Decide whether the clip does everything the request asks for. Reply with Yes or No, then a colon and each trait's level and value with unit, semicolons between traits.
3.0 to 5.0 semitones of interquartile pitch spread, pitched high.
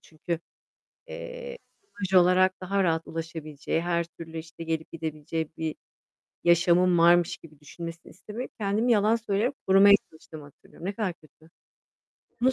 No: average, 3.5 semitones; medium, 170 Hz